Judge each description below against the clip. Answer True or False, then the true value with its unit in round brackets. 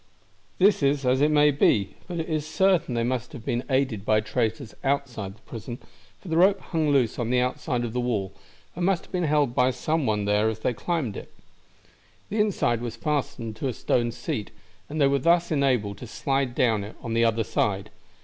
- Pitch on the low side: True (125 Hz)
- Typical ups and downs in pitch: True (4.8 semitones)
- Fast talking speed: True (215 wpm)